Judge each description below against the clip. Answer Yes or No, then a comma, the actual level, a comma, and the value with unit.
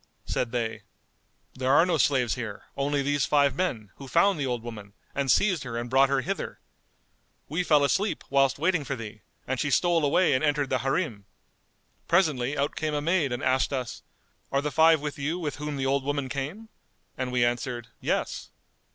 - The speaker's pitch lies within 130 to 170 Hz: Yes, medium, 140 Hz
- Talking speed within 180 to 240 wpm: Yes, average, 190 wpm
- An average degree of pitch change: Yes, average, 3.1 semitones